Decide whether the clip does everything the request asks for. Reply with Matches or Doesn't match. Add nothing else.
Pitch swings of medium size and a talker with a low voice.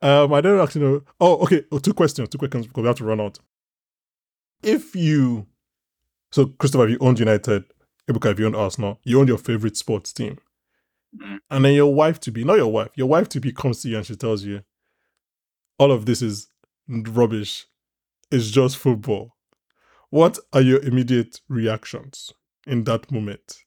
Matches